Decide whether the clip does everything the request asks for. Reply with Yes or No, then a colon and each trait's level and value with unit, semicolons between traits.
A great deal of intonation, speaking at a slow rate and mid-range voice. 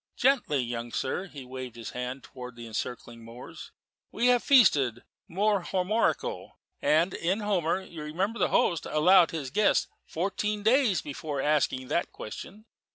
No: wide, 7.7 semitones; average, 150 wpm; medium, 160 Hz